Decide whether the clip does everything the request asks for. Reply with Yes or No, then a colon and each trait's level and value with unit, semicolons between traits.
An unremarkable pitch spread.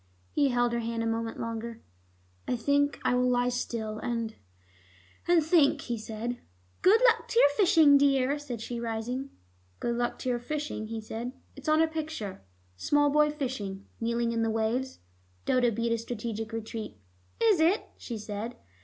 Yes: average, 4.0 semitones